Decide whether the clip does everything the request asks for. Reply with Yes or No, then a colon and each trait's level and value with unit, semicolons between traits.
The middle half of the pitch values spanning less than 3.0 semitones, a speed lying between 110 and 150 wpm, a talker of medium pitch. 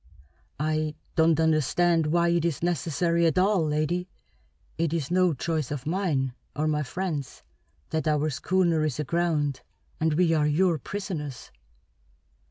Yes: narrow, 2.4 semitones; average, 140 wpm; medium, 160 Hz